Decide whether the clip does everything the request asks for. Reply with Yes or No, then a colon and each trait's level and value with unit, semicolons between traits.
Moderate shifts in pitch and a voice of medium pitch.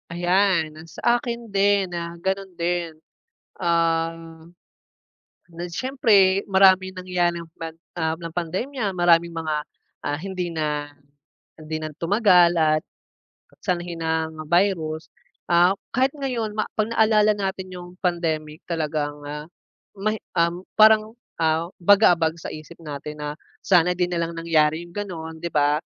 Yes: average, 3.2 semitones; medium, 170 Hz